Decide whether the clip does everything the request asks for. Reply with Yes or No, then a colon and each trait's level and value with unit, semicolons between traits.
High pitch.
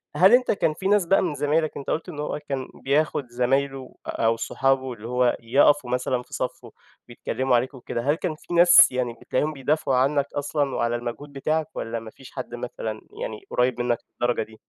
No: low, 135 Hz